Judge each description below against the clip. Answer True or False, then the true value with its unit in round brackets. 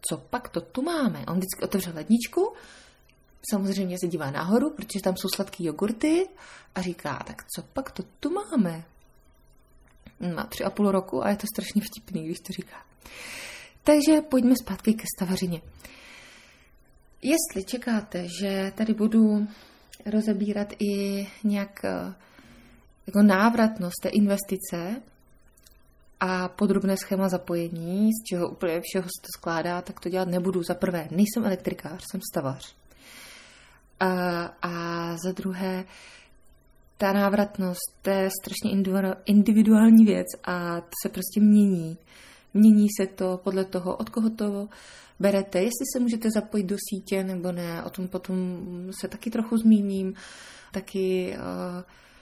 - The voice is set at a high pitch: True (195 Hz)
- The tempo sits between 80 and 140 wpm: True (135 wpm)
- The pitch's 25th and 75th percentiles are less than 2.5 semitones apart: False (2.8 semitones)